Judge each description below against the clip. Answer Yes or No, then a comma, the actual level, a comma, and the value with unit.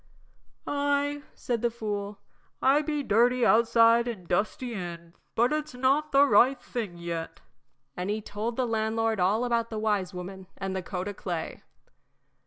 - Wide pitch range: No, average, 4.4 semitones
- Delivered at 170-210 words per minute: No, average, 160 wpm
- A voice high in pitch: Yes, high, 225 Hz